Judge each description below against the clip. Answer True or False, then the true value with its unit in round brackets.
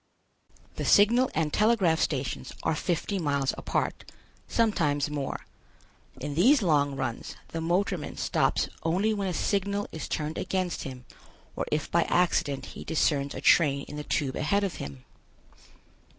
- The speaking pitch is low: False (160 Hz)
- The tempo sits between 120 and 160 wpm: True (150 wpm)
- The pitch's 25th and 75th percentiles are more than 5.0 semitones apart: True (5.5 semitones)